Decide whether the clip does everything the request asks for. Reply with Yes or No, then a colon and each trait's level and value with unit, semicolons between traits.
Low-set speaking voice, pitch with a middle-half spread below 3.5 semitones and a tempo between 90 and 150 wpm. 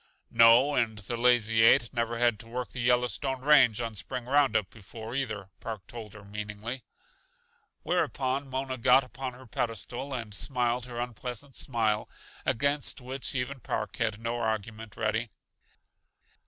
Yes: low, 120 Hz; narrow, 2.6 semitones; average, 145 wpm